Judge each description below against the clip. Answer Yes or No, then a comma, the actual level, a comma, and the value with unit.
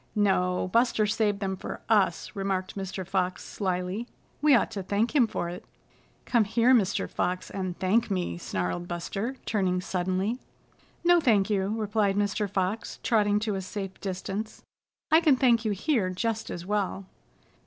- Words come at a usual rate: Yes, average, 160 wpm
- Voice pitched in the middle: No, high, 200 Hz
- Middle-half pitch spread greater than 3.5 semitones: No, average, 3.2 semitones